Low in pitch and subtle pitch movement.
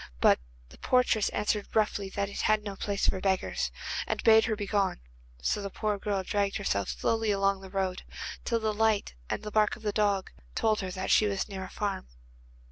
No: high, 205 Hz; narrow, 1.8 semitones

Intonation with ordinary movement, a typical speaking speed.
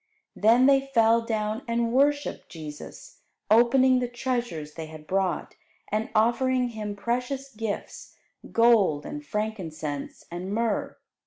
No: average, 4.2 semitones; slow, 125 wpm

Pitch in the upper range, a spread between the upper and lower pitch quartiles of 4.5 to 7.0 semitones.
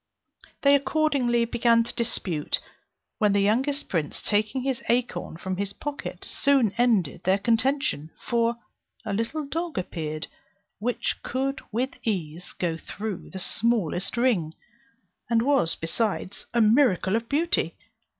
Yes: high, 230 Hz; wide, 5.5 semitones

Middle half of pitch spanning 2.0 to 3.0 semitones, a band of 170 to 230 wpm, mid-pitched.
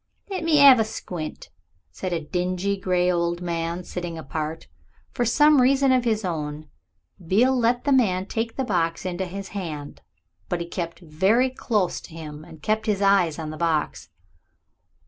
No: average, 5.2 semitones; average, 180 wpm; medium, 180 Hz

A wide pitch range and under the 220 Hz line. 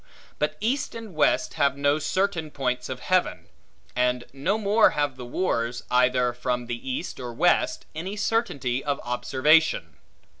Yes: wide, 6.7 semitones; medium, 140 Hz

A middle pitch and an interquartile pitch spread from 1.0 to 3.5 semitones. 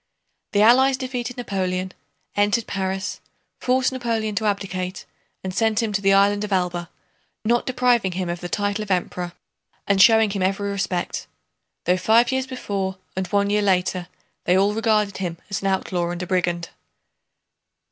No: high, 200 Hz; average, 3.1 semitones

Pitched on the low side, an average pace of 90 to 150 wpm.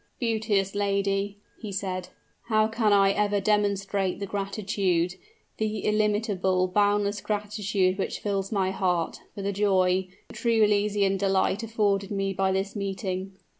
No: high, 200 Hz; slow, 135 wpm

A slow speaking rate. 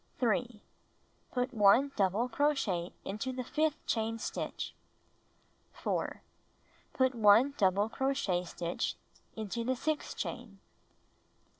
Yes: slow, 115 wpm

